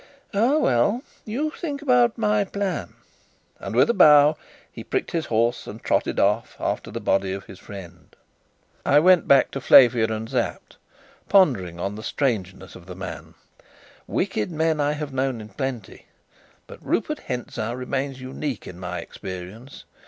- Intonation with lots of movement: Yes, wide, 8.2 semitones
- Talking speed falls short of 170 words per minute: Yes, average, 155 wpm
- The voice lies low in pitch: Yes, low, 130 Hz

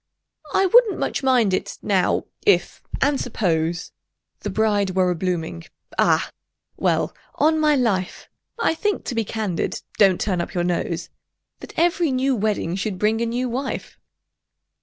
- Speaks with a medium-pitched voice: No, high, 215 Hz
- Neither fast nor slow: No, slow, 130 wpm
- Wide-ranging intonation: Yes, wide, 6.5 semitones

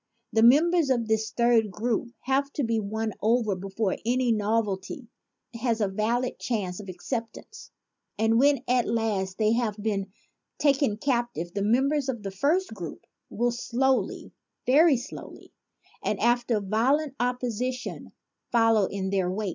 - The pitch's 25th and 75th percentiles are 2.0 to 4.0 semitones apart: Yes, average, 3.3 semitones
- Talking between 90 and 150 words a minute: Yes, average, 145 wpm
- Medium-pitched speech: No, high, 230 Hz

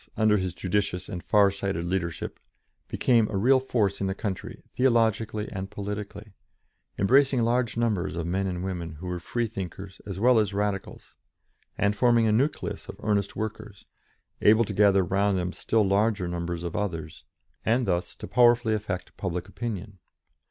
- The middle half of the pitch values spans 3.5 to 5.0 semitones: No, average, 3.0 semitones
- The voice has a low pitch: Yes, low, 100 Hz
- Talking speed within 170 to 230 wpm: No, average, 160 wpm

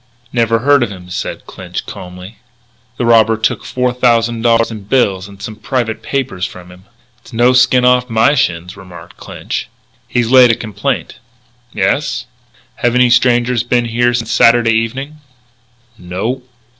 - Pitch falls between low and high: No, low, 115 Hz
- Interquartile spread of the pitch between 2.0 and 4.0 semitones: Yes, average, 3.4 semitones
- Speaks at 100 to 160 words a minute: Yes, average, 155 wpm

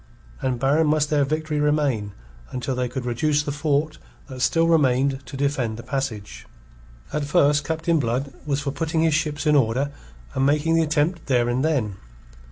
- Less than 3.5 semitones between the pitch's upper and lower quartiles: Yes, average, 2.9 semitones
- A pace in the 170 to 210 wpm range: Yes, average, 175 wpm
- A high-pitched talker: No, medium, 145 Hz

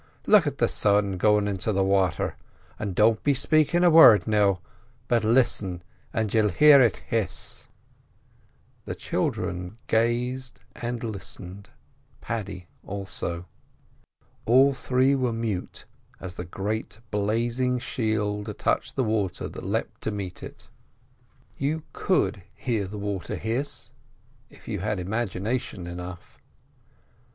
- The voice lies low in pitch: Yes, low, 105 Hz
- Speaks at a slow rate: Yes, slow, 125 wpm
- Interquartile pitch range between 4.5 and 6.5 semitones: No, average, 3.7 semitones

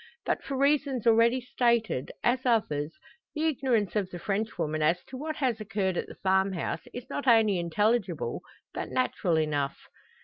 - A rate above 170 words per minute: No, average, 160 wpm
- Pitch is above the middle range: Yes, high, 220 Hz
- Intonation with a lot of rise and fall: Yes, wide, 6.1 semitones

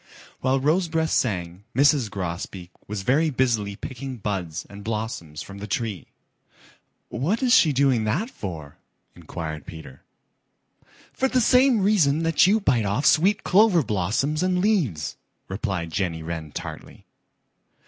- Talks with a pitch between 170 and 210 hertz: No, low, 115 Hz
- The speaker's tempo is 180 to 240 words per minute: No, slow, 135 wpm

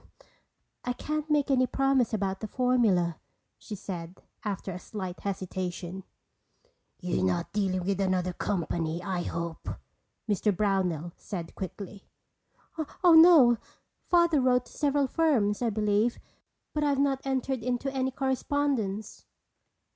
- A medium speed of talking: No, slow, 125 wpm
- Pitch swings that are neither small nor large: No, wide, 6.3 semitones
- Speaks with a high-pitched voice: Yes, high, 210 Hz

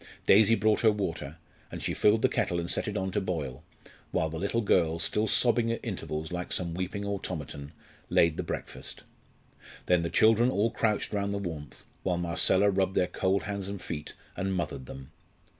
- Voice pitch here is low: Yes, very low, 95 Hz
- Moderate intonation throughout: Yes, average, 3.8 semitones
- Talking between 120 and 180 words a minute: No, average, 190 wpm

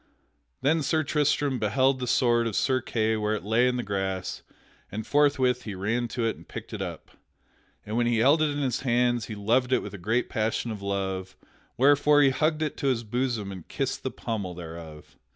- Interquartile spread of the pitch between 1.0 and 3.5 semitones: No, average, 4.2 semitones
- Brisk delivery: Yes, fast, 210 wpm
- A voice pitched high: No, low, 120 Hz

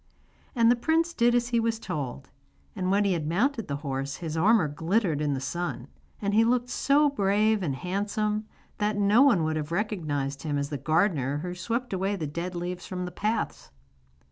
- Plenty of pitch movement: Yes, wide, 6.1 semitones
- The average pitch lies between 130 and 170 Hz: No, medium, 185 Hz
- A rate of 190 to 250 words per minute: Yes, average, 195 wpm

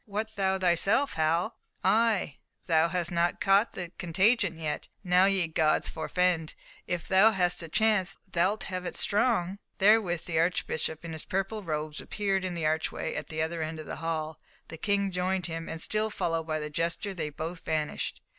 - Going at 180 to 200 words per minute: Yes, average, 185 wpm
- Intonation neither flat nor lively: Yes, average, 3.3 semitones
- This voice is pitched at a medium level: Yes, medium, 175 Hz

